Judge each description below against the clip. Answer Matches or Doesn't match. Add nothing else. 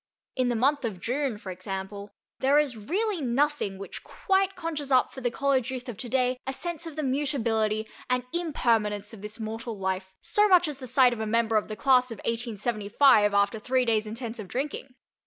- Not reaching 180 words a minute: Doesn't match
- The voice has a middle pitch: Doesn't match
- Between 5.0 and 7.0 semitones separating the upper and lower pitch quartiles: Doesn't match